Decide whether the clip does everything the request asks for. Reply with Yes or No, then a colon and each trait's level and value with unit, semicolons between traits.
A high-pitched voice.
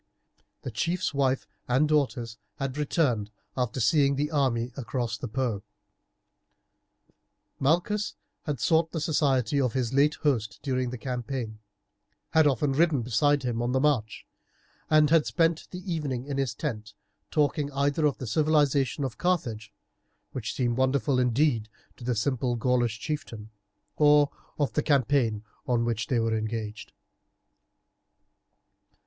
No: low, 130 Hz